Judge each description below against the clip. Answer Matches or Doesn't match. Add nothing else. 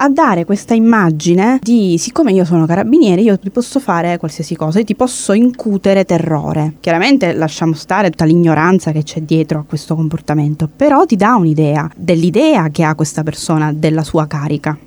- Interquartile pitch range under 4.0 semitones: Doesn't match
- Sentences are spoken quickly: Matches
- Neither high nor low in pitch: Matches